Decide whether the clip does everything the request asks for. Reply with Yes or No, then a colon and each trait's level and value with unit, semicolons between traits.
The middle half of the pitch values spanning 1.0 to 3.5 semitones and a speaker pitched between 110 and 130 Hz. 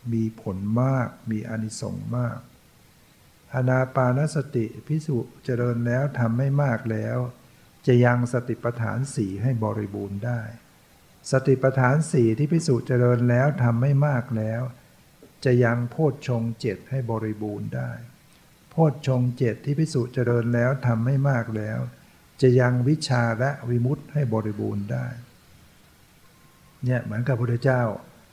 Yes: average, 2.7 semitones; low, 120 Hz